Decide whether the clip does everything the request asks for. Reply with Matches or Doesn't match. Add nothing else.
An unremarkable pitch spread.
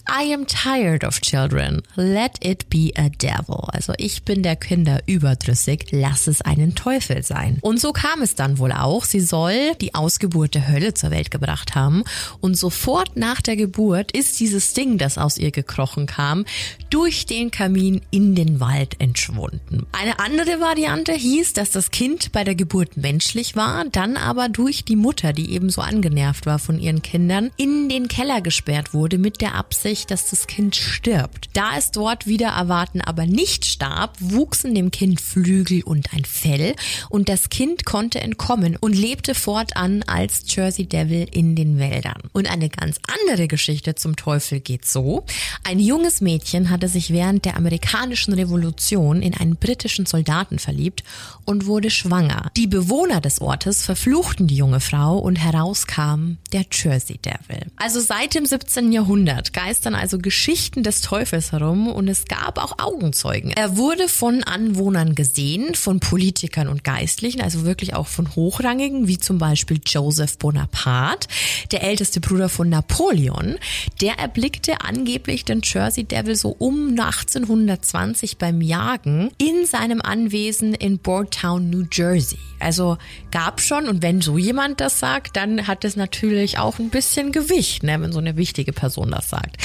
Doesn't match